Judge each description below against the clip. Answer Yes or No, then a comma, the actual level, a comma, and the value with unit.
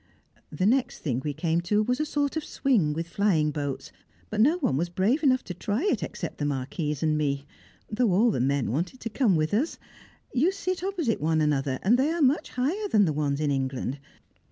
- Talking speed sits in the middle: No, fast, 215 wpm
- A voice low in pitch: No, medium, 185 Hz